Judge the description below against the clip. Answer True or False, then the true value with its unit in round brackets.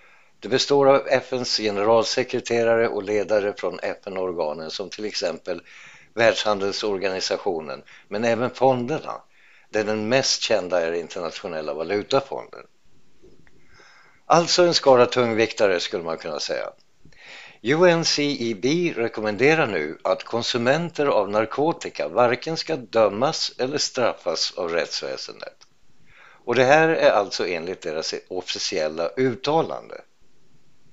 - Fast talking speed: False (105 wpm)